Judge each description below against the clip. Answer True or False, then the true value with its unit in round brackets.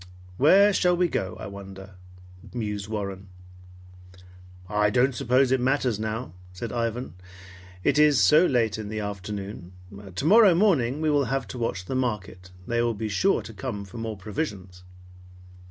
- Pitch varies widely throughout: False (4.9 semitones)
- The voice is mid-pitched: False (115 Hz)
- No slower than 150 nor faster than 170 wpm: True (155 wpm)